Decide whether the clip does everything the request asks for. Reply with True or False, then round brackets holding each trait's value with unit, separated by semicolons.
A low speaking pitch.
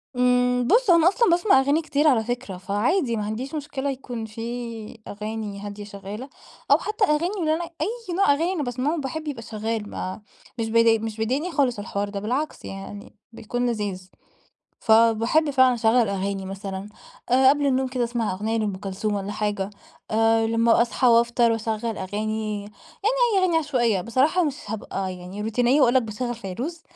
False (230 Hz)